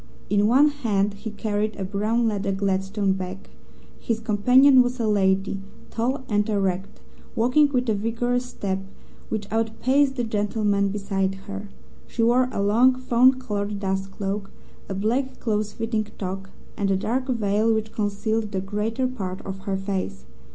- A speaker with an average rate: Yes, average, 160 wpm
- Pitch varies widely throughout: No, average, 3.1 semitones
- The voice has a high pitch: Yes, high, 210 Hz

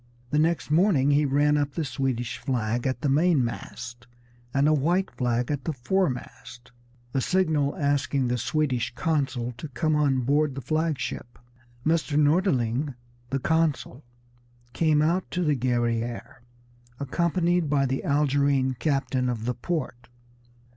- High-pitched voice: No, medium, 140 Hz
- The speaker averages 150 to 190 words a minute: No, average, 140 wpm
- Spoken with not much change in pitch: No, average, 3.7 semitones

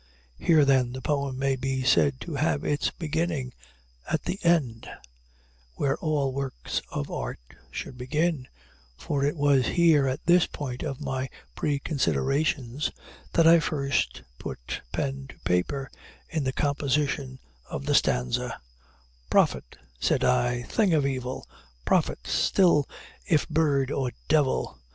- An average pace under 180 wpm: Yes, slow, 135 wpm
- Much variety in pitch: No, average, 2.8 semitones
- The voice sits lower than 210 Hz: Yes, medium, 140 Hz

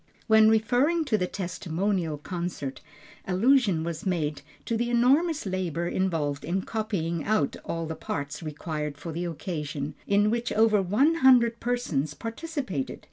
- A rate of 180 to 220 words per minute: No, average, 140 wpm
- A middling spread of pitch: No, wide, 6.3 semitones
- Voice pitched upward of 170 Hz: Yes, medium, 185 Hz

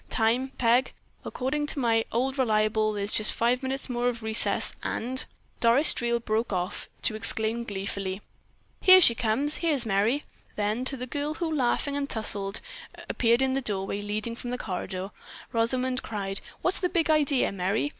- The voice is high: Yes, high, 235 Hz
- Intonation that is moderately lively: Yes, average, 3.7 semitones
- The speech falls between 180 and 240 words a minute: No, average, 165 wpm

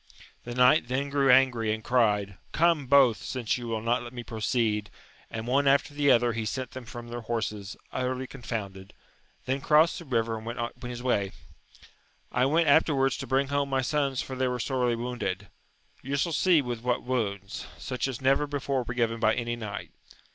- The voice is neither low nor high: No, low, 125 Hz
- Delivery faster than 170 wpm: Yes, average, 195 wpm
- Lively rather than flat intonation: No, average, 2.8 semitones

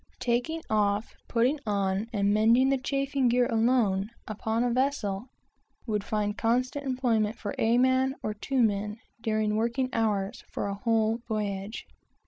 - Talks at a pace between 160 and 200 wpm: No, average, 140 wpm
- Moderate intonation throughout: Yes, average, 3.3 semitones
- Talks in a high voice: Yes, high, 225 Hz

